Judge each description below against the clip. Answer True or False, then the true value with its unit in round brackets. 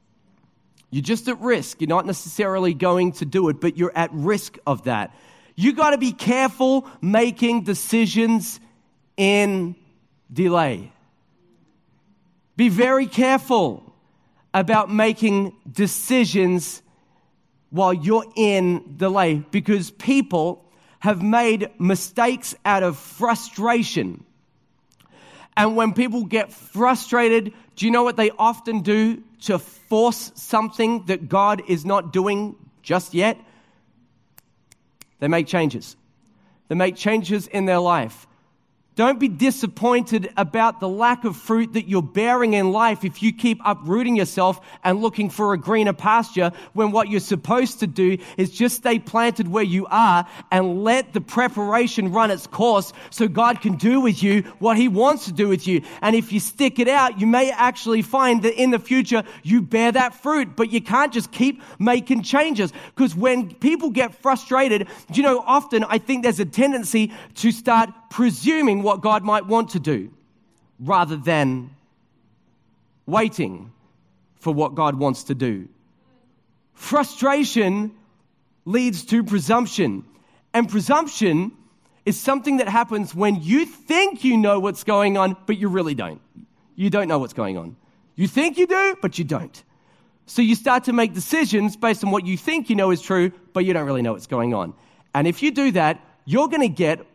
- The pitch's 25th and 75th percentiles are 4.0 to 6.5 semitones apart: True (4.5 semitones)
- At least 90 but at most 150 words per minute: False (160 wpm)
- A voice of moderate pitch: False (210 Hz)